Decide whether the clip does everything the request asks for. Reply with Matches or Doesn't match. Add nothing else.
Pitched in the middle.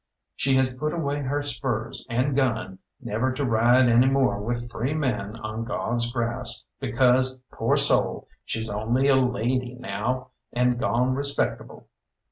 Doesn't match